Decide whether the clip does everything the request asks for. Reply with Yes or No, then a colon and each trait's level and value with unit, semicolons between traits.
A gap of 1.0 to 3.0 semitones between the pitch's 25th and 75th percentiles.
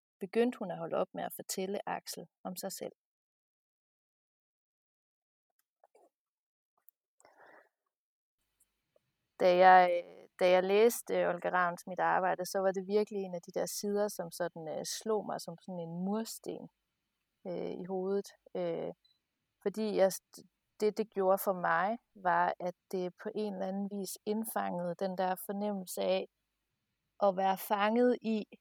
Yes: narrow, 2.6 semitones